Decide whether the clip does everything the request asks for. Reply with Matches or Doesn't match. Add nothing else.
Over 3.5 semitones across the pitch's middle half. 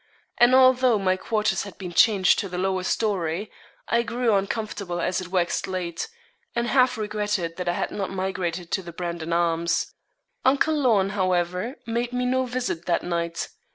Matches